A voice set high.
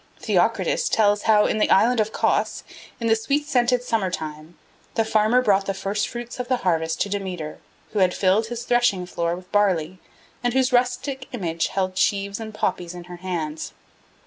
Yes: high, 205 Hz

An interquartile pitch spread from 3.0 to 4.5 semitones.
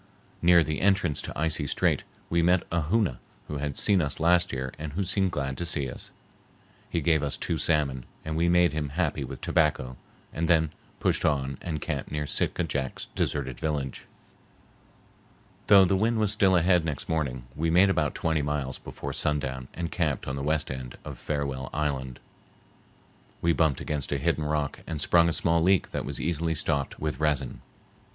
Yes: average, 3.4 semitones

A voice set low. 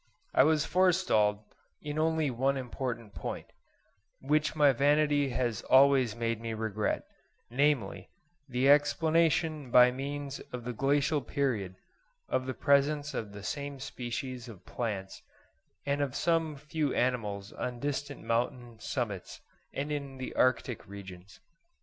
Yes: low, 130 Hz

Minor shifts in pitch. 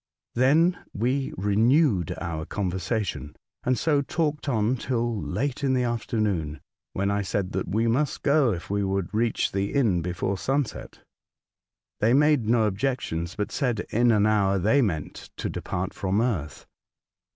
No: average, 5.1 semitones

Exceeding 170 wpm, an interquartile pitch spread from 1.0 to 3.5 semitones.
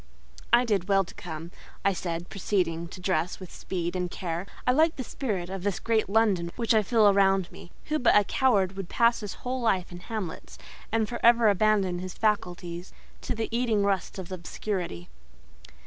No: average, 190 wpm; average, 3.9 semitones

